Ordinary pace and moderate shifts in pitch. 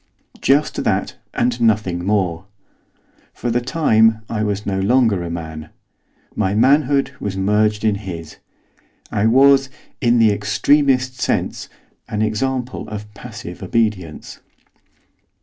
No: slow, 120 wpm; average, 3.9 semitones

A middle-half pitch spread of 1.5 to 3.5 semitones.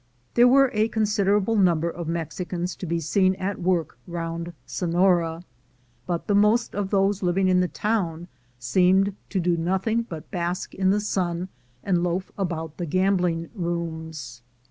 Yes: narrow, 2.6 semitones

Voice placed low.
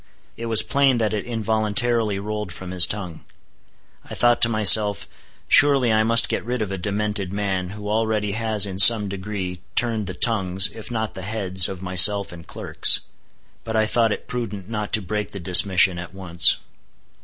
Yes: low, 105 Hz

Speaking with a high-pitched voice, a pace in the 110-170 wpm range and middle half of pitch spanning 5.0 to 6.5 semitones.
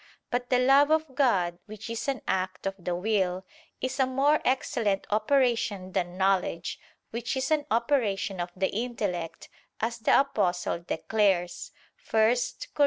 Yes: high, 220 Hz; average, 150 wpm; wide, 5.5 semitones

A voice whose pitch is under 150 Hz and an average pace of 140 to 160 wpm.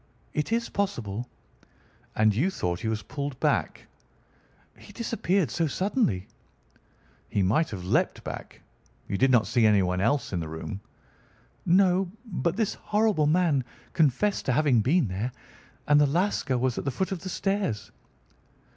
Yes: medium, 140 Hz; average, 155 wpm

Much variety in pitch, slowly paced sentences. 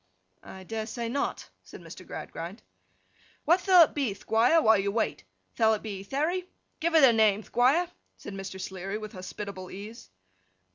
No: wide, 5.9 semitones; average, 170 wpm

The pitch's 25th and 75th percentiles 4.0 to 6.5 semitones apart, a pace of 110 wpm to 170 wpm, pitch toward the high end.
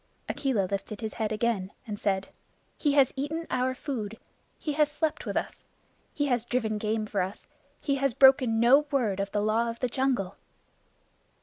No: average, 4.5 semitones; average, 180 wpm; high, 235 Hz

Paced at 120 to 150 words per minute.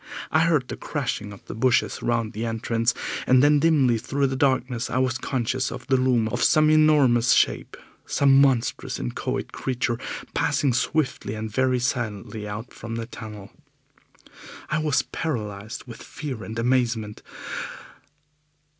Yes: average, 145 wpm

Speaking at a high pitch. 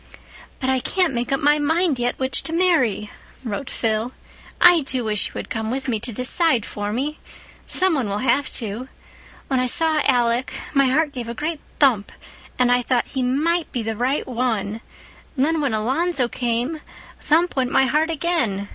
Yes: very high, 260 Hz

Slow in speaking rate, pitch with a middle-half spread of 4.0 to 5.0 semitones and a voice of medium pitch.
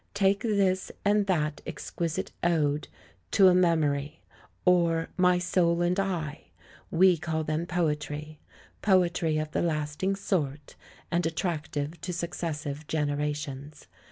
No: slow, 120 wpm; average, 3.1 semitones; medium, 165 Hz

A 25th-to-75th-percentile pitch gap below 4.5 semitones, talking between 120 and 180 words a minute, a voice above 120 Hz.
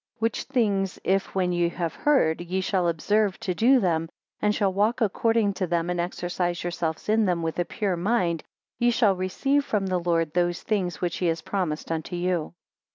No: average, 3.3 semitones; average, 200 wpm; medium, 185 Hz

